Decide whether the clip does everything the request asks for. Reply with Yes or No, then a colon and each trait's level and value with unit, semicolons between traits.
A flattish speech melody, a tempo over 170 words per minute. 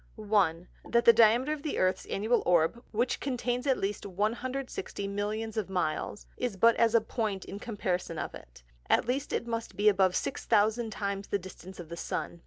No: average, 3.7 semitones; average, 190 wpm